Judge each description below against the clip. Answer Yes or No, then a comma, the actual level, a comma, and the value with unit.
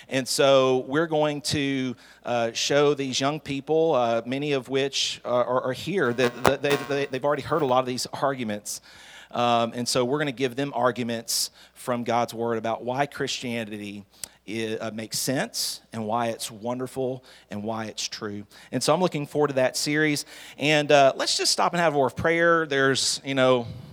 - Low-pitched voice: Yes, low, 130 Hz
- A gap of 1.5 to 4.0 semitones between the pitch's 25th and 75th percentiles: Yes, average, 3.5 semitones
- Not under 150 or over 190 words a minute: No, average, 200 wpm